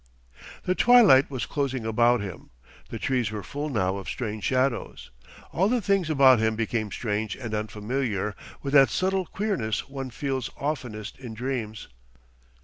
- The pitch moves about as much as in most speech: Yes, average, 4.4 semitones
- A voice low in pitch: Yes, low, 125 Hz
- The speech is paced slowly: No, average, 150 wpm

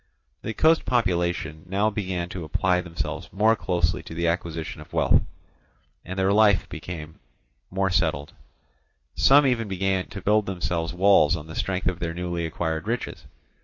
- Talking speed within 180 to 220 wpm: No, average, 160 wpm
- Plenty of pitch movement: No, average, 3.1 semitones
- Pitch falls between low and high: No, very low, 90 Hz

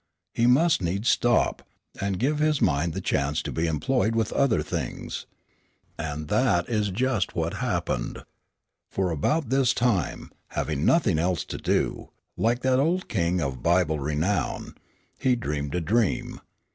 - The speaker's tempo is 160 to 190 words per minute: No, average, 150 wpm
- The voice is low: Yes, very low, 95 Hz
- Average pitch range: No, wide, 7.7 semitones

